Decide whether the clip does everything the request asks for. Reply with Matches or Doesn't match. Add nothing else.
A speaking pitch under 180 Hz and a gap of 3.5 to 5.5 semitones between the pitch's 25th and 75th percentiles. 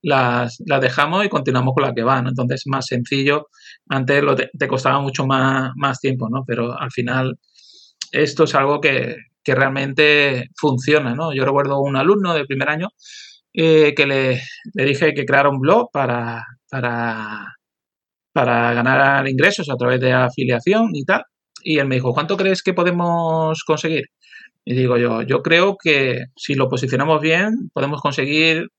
Doesn't match